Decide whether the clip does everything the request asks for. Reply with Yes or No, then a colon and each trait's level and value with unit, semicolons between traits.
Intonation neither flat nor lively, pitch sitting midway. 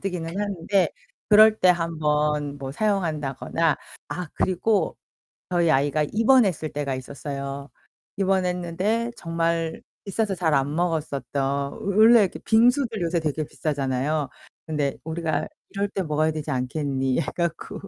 Yes: average, 4.8 semitones; medium, 165 Hz